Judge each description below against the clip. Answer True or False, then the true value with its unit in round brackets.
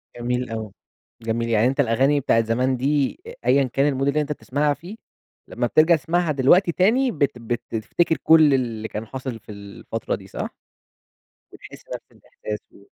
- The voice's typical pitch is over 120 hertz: True (135 Hz)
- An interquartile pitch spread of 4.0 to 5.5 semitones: True (4.7 semitones)